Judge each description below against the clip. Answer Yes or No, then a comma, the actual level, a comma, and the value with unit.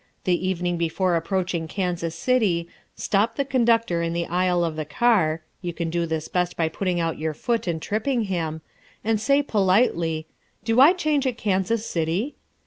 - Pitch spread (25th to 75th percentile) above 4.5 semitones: Yes, average, 5.2 semitones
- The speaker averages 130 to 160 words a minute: No, average, 175 wpm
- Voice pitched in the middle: Yes, medium, 180 Hz